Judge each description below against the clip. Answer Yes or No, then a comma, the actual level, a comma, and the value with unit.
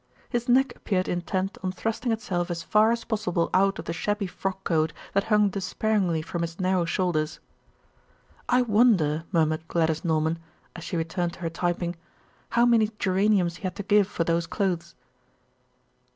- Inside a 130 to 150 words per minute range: No, average, 165 wpm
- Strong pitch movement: No, average, 3.7 semitones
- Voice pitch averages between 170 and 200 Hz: Yes, medium, 185 Hz